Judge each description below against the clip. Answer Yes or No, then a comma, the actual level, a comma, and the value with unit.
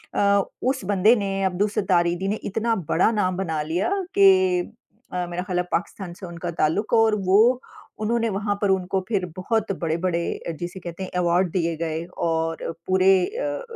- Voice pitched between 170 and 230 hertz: Yes, medium, 185 Hz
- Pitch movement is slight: No, average, 3.0 semitones